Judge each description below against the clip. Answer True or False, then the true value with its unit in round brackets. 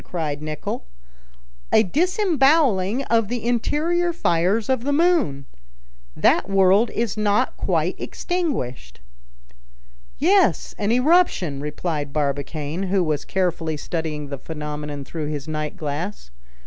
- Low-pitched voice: False (185 Hz)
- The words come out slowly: True (115 wpm)